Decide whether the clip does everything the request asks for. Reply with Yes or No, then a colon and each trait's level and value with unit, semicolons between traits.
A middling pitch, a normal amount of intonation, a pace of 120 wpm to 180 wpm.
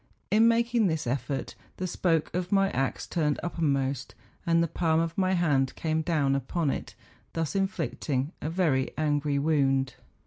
Yes: medium, 160 Hz; average, 4.1 semitones; average, 160 wpm